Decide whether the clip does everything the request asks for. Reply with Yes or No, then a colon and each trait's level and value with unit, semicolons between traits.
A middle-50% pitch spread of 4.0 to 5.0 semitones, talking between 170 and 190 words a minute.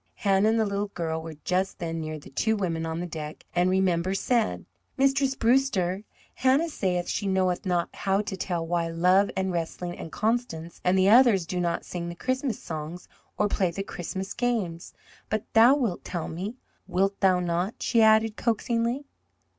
Yes: average, 4.3 semitones; average, 180 wpm